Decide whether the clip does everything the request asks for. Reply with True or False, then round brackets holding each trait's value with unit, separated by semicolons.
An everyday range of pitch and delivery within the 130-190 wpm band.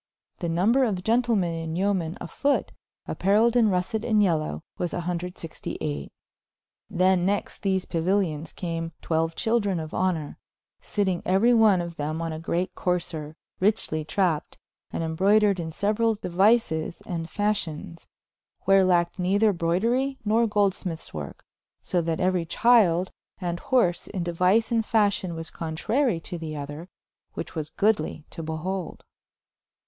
True (3.9 semitones; 140 wpm)